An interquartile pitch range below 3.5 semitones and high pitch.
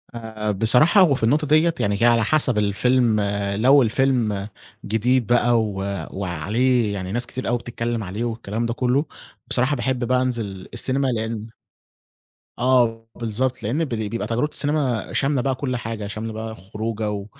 No: average, 3.1 semitones; low, 115 Hz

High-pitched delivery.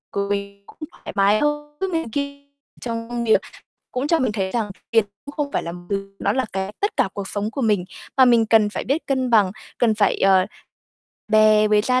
Yes: high, 225 Hz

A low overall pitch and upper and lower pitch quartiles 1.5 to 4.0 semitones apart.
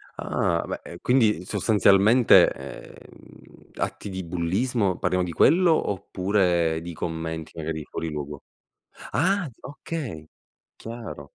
No: very low, 90 Hz; wide, 6.3 semitones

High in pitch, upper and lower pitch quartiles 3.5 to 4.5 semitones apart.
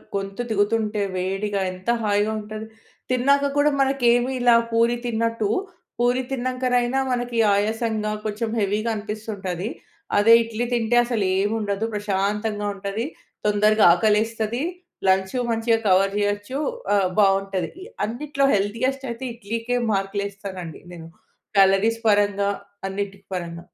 No: high, 210 Hz; average, 2.8 semitones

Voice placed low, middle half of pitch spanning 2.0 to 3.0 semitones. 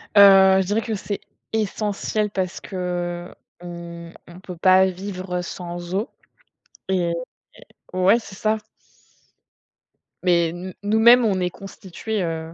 No: medium, 185 Hz; narrow, 2.5 semitones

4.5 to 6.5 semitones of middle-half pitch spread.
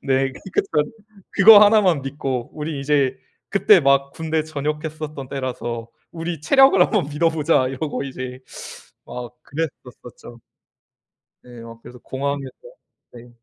No: average, 3.5 semitones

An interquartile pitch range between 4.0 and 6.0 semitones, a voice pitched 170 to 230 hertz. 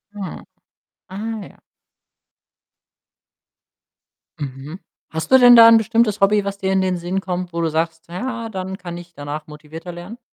Yes: average, 4.3 semitones; medium, 185 Hz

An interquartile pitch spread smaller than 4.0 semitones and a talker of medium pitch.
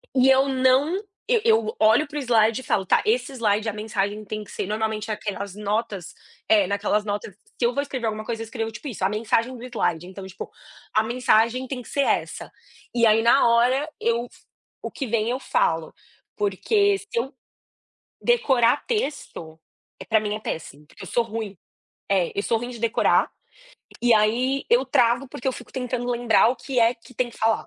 No: average, 3.3 semitones; high, 230 Hz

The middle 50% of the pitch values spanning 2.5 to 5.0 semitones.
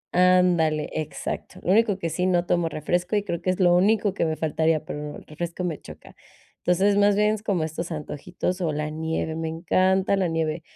Yes: average, 2.8 semitones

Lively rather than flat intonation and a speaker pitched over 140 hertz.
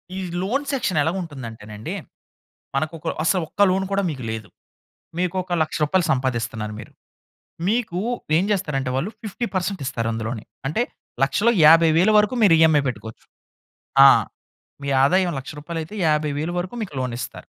Yes: wide, 6.4 semitones; medium, 160 Hz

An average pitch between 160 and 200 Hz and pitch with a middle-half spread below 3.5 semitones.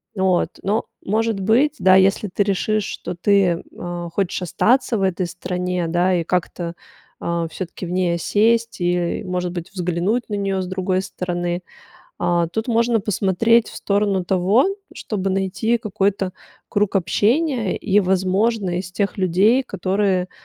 Yes: high, 190 Hz; average, 2.8 semitones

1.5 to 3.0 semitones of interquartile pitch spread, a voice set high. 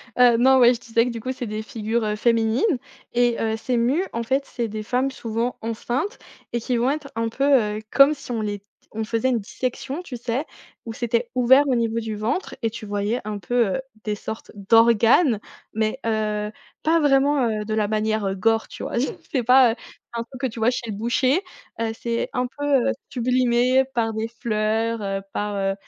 Yes: narrow, 2.5 semitones; high, 230 Hz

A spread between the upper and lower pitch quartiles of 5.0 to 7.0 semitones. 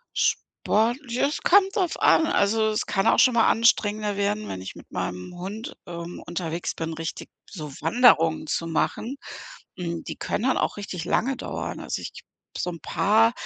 Yes: wide, 5.5 semitones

